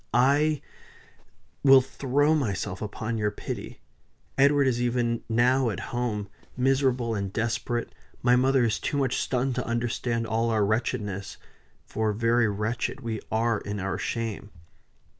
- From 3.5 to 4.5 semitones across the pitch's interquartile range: No, average, 2.9 semitones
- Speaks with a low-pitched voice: Yes, low, 120 Hz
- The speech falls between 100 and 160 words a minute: Yes, average, 140 wpm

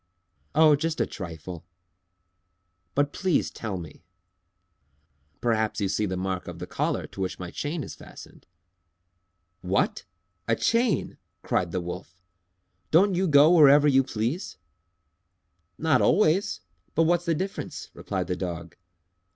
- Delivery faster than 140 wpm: No, slow, 135 wpm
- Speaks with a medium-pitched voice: No, low, 130 Hz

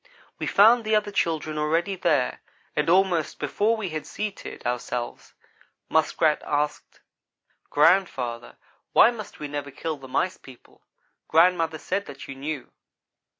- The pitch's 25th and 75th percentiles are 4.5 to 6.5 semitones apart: Yes, average, 5.0 semitones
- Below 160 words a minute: Yes, slow, 135 wpm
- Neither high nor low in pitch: Yes, medium, 160 Hz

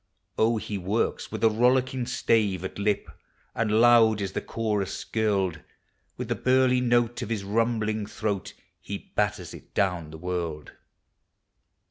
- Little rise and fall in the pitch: No, average, 3.0 semitones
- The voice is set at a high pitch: No, low, 105 Hz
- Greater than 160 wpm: No, average, 145 wpm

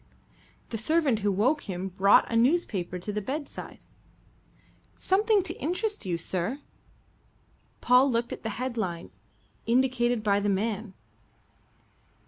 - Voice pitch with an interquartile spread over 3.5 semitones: Yes, average, 5.3 semitones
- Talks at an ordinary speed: No, slow, 120 wpm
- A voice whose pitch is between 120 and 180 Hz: No, high, 230 Hz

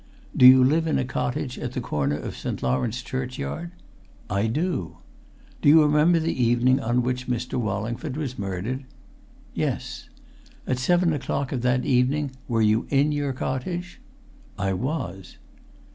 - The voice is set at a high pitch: No, low, 125 Hz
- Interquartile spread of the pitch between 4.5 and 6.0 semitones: No, average, 3.9 semitones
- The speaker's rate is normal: Yes, average, 150 wpm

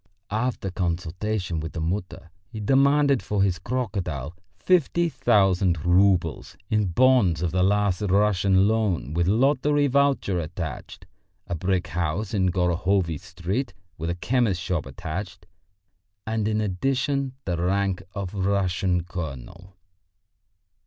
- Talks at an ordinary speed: No, slow, 125 wpm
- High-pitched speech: No, very low, 95 Hz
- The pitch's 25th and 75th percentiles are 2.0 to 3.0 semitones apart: No, average, 3.7 semitones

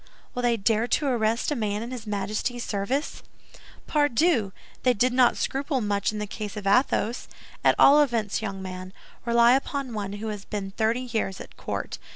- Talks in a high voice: Yes, high, 225 Hz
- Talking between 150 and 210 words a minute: Yes, average, 185 wpm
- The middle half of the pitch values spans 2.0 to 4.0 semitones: Yes, average, 3.5 semitones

